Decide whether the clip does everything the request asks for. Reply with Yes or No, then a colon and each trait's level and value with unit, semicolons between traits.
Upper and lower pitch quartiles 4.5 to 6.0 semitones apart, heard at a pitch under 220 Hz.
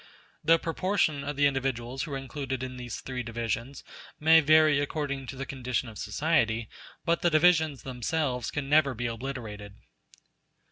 No: average, 3.9 semitones; low, 135 Hz